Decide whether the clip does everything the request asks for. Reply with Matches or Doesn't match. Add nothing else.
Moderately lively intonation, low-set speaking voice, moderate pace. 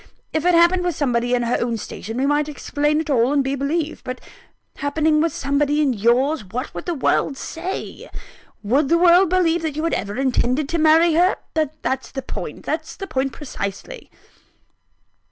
Doesn't match